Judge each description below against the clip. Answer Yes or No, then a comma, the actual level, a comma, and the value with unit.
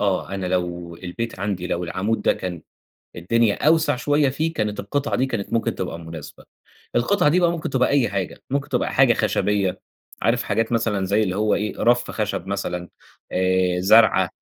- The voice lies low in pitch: Yes, low, 105 Hz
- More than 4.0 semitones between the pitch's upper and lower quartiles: Yes, average, 4.8 semitones